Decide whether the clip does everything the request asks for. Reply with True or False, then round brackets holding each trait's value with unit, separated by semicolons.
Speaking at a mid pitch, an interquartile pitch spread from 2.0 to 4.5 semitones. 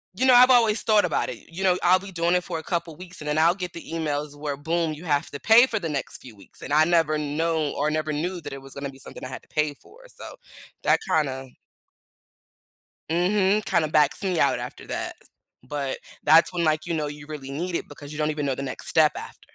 True (155 Hz; 3.4 semitones)